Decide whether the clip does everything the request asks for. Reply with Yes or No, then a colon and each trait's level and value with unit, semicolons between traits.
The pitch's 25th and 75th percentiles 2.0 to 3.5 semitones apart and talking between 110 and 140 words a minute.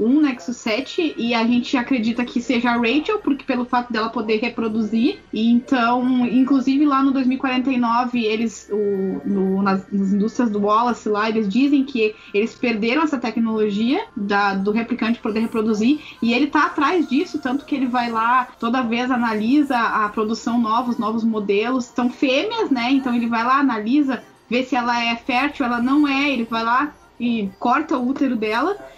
No: average, 3.1 semitones; average, 180 wpm